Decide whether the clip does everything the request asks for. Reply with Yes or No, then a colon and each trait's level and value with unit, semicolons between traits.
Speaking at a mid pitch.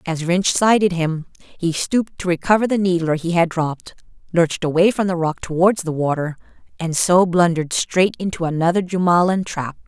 Yes: medium, 175 Hz